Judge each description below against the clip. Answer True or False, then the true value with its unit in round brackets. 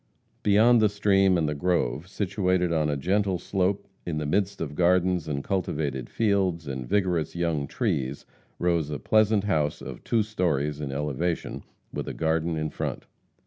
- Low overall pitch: True (85 Hz)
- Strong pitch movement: False (4.6 semitones)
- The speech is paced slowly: False (165 wpm)